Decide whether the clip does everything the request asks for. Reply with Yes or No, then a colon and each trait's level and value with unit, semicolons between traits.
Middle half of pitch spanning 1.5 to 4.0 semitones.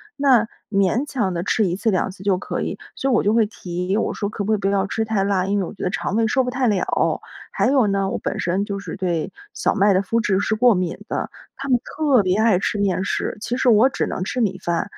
Yes: average, 3.4 semitones